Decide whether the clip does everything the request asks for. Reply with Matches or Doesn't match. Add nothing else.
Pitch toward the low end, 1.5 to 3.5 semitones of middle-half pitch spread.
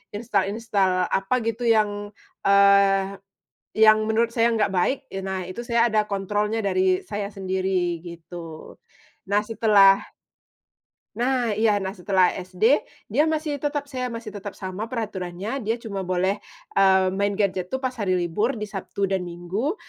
Doesn't match